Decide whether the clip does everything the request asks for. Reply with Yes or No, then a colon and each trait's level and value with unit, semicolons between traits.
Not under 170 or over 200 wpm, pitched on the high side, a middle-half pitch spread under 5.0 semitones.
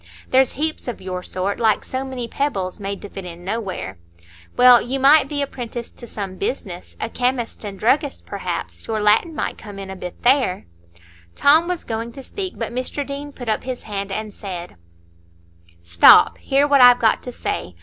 No: average, 185 wpm; high, 235 Hz; average, 5.3 semitones